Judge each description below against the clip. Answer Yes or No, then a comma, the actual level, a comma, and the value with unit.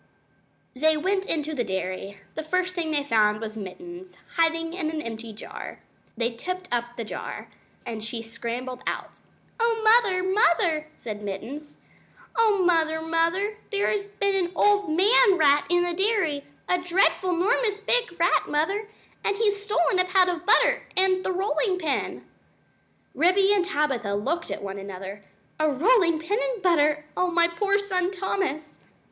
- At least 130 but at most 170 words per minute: Yes, average, 160 wpm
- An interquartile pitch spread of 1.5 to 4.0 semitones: No, average, 5.3 semitones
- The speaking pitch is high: Yes, very high, 340 Hz